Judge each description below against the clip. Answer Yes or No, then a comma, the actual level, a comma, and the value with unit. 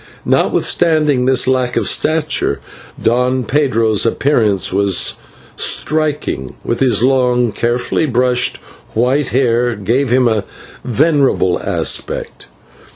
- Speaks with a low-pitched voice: Yes, low, 125 Hz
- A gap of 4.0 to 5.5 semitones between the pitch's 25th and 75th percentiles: No, average, 3.0 semitones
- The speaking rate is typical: No, slow, 100 wpm